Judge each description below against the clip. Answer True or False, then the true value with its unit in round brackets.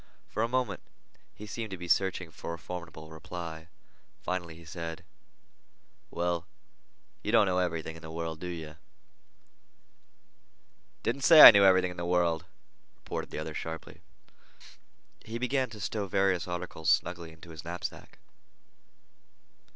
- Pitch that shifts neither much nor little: True (3.1 semitones)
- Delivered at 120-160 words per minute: True (145 wpm)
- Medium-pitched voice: False (90 Hz)